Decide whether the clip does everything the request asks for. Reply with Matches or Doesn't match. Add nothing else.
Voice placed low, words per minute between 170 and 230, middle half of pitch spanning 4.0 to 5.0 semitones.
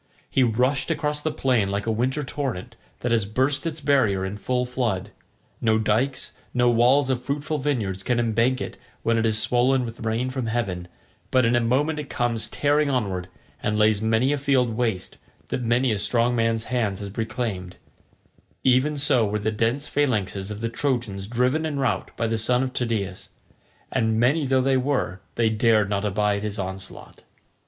Doesn't match